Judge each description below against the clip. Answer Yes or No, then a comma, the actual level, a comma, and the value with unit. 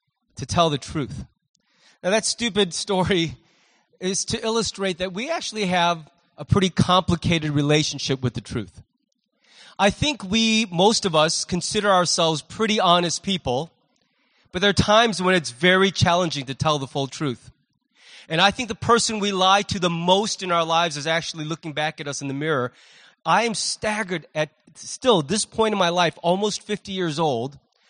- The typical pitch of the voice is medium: Yes, medium, 180 Hz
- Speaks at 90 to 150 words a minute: No, average, 175 wpm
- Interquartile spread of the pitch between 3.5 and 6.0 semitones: Yes, average, 5.0 semitones